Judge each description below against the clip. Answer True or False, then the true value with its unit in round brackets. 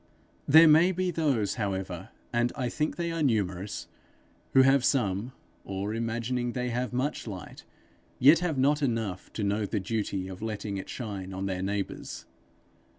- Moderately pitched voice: False (115 Hz)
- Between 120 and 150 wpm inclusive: False (160 wpm)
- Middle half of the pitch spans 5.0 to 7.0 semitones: True (5.4 semitones)